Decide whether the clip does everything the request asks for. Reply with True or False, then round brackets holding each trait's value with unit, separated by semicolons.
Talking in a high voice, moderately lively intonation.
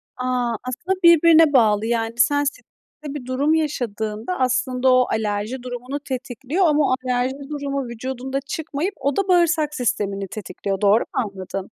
True (255 Hz; 4.0 semitones)